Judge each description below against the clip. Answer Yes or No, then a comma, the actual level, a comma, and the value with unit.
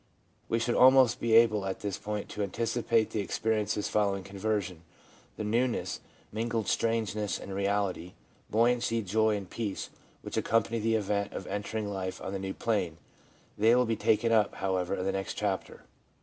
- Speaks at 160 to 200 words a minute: Yes, average, 165 wpm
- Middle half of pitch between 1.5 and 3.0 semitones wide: Yes, narrow, 2.6 semitones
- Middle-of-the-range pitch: No, low, 105 Hz